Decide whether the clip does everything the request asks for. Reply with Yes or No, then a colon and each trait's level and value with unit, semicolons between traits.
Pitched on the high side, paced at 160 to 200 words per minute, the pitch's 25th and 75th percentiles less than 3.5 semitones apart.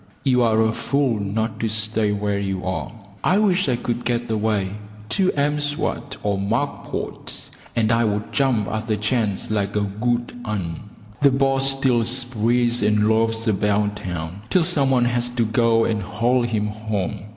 No: low, 115 Hz; average, 175 wpm; average, 2.9 semitones